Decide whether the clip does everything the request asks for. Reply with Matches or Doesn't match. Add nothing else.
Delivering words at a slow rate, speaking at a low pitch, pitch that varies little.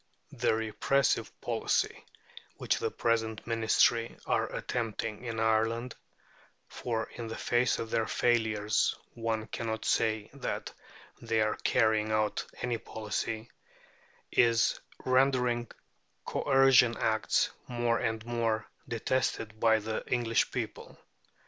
Matches